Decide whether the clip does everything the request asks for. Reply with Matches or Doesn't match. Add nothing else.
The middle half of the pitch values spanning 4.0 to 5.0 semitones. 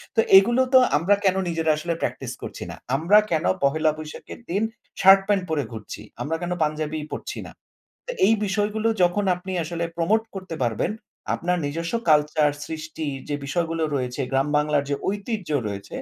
Matches